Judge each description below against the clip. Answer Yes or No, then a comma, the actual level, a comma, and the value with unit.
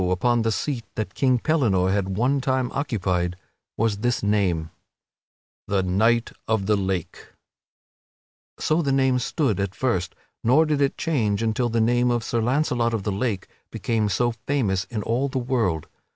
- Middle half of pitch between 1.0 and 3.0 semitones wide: No, average, 4.5 semitones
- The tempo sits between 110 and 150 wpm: No, average, 165 wpm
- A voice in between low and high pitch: No, low, 115 Hz